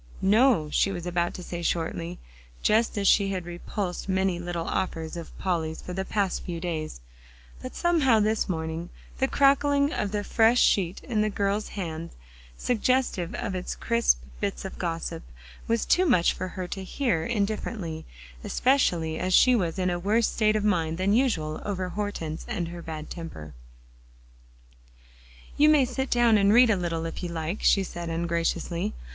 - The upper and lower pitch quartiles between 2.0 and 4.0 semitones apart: No, average, 4.4 semitones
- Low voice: No, medium, 185 Hz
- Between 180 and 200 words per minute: No, average, 170 wpm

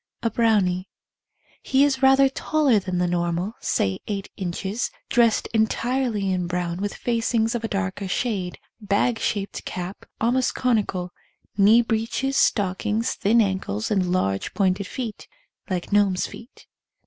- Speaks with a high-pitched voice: Yes, high, 205 Hz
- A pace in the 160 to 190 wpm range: No, average, 140 wpm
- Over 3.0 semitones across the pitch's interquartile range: Yes, average, 4.1 semitones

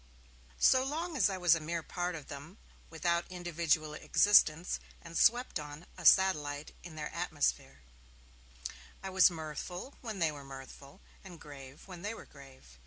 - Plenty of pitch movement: No, average, 3.9 semitones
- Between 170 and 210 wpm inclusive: No, average, 160 wpm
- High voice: No, medium, 170 Hz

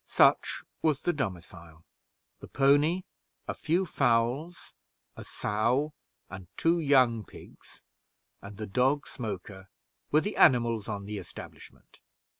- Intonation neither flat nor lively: No, wide, 6.5 semitones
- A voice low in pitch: Yes, low, 120 Hz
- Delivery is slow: Yes, slow, 120 wpm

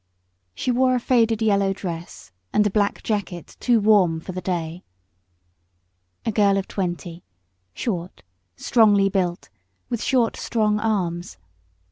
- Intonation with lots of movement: No, average, 3.9 semitones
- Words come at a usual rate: No, slow, 130 wpm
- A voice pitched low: No, high, 200 Hz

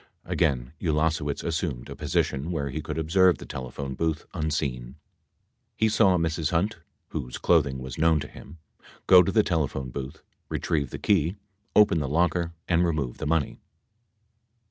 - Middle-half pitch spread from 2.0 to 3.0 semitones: No, average, 3.5 semitones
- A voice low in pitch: Yes, very low, 80 Hz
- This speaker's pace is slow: No, average, 155 wpm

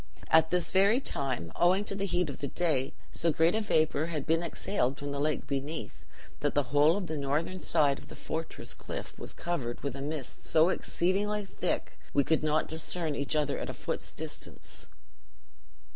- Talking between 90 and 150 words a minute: No, average, 190 wpm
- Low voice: No, medium, 160 Hz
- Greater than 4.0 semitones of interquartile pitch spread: No, average, 3.7 semitones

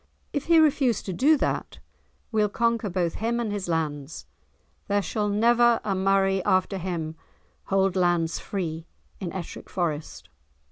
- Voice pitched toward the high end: Yes, high, 195 Hz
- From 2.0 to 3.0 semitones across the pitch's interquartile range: No, average, 4.8 semitones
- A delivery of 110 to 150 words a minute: Yes, average, 145 wpm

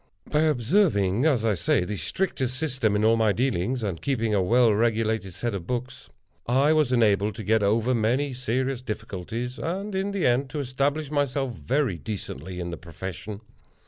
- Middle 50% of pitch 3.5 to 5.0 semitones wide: Yes, average, 4.7 semitones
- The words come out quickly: No, average, 175 wpm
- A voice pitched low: Yes, low, 120 Hz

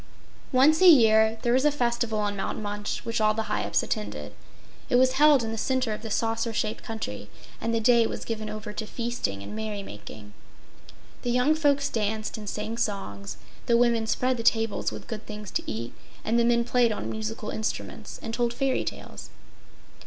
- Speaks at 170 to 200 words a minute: Yes, average, 195 wpm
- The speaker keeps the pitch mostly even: Yes, narrow, 2.2 semitones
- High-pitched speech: Yes, high, 225 Hz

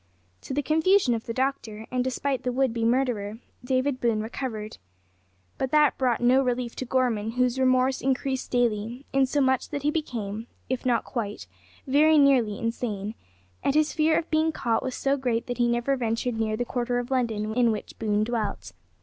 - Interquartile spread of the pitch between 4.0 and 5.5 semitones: No, average, 2.8 semitones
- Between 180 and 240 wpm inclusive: Yes, average, 185 wpm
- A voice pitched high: Yes, very high, 250 Hz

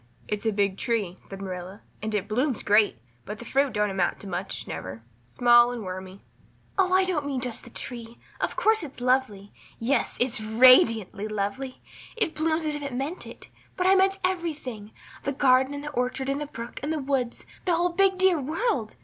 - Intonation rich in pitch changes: Yes, wide, 6.0 semitones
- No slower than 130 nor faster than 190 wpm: No, average, 200 wpm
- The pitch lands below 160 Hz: No, very high, 250 Hz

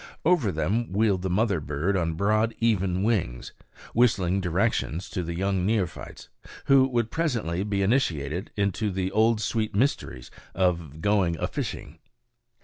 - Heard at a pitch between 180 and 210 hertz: No, low, 100 Hz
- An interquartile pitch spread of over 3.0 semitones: Yes, average, 4.1 semitones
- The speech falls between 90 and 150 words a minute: Yes, average, 140 wpm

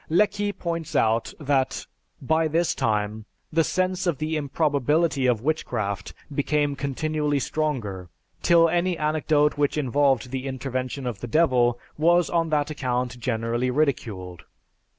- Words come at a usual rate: No, slow, 130 wpm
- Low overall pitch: No, medium, 145 Hz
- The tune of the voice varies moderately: Yes, average, 4.3 semitones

